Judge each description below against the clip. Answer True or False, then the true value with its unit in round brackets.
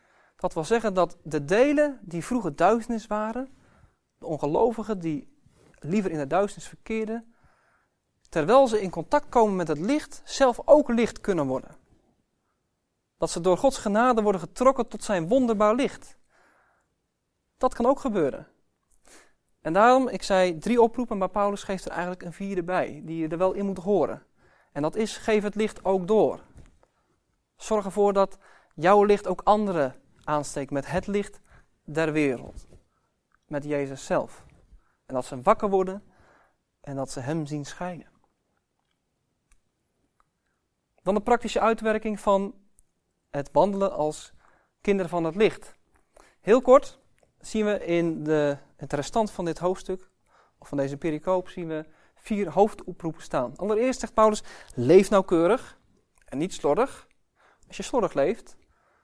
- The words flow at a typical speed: True (145 wpm)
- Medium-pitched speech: False (195 Hz)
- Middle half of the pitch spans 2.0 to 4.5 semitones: False (5.0 semitones)